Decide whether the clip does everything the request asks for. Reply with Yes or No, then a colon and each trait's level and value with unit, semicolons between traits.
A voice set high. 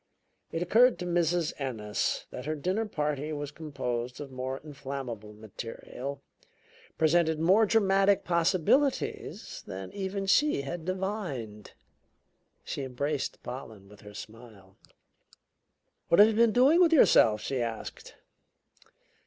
No: medium, 150 Hz